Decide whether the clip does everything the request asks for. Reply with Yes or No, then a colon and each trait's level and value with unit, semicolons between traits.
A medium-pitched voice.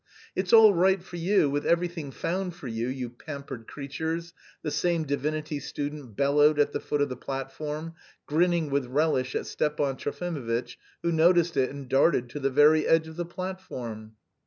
Yes: medium, 150 Hz